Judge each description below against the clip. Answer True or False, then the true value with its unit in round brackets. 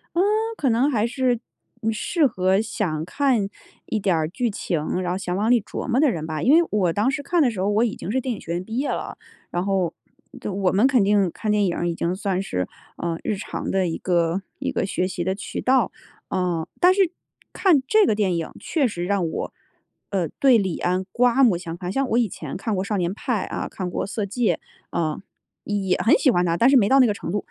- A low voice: False (200 Hz)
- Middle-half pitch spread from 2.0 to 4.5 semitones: False (5.4 semitones)